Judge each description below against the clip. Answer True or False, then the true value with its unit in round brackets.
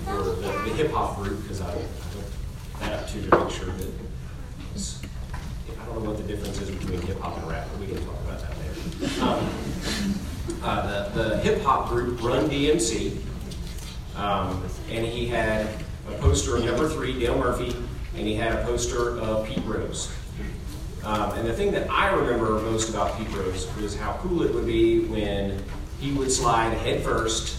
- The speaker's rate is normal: True (180 wpm)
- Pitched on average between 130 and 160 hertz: False (100 Hz)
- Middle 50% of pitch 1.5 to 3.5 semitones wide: False (4.1 semitones)